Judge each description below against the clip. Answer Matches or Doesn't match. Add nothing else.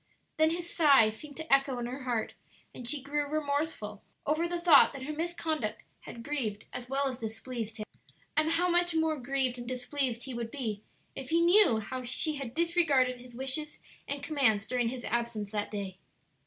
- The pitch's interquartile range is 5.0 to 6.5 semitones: Doesn't match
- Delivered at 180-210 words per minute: Matches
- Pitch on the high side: Matches